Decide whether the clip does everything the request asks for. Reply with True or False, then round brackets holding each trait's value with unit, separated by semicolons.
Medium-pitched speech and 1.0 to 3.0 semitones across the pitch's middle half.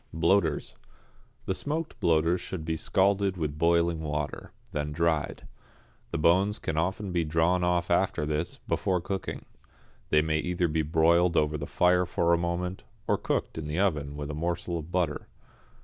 False (85 Hz; 2.5 semitones)